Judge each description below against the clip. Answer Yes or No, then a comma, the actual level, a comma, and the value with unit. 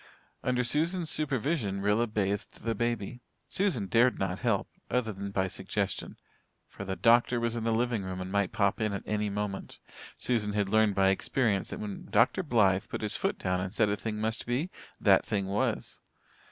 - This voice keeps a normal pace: Yes, average, 190 wpm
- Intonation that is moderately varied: Yes, average, 3.3 semitones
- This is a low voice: Yes, low, 105 Hz